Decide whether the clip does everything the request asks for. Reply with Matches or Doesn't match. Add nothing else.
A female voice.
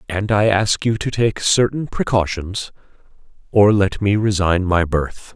Doesn't match